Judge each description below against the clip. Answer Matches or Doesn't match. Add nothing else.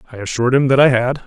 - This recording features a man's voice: Matches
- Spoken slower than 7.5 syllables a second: Doesn't match